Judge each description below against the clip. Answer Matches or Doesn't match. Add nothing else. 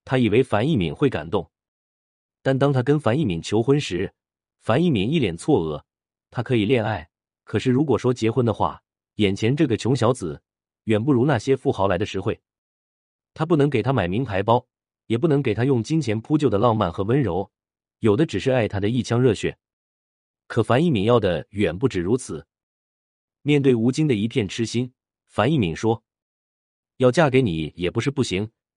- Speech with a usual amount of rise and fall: Doesn't match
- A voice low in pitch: Matches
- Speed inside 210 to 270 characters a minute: Matches